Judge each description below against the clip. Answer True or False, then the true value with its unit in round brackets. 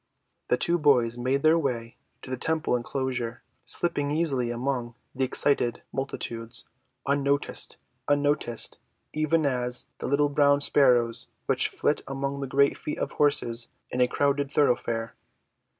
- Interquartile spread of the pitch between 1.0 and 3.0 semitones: True (2.7 semitones)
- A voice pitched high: False (135 Hz)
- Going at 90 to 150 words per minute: True (135 wpm)